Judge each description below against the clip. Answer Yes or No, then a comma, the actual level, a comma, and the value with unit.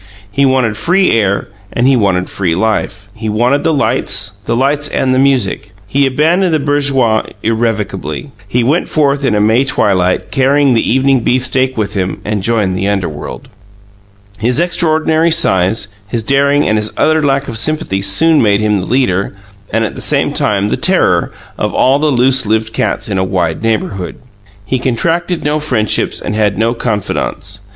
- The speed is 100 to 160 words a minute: No, average, 175 wpm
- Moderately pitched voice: No, low, 115 Hz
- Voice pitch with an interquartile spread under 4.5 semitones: No, average, 5.2 semitones